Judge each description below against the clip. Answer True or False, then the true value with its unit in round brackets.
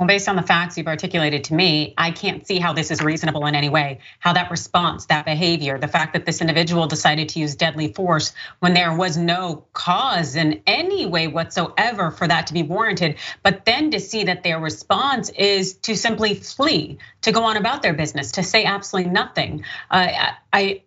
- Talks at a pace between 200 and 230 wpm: True (205 wpm)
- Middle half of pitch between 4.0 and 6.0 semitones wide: False (3.6 semitones)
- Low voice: False (170 Hz)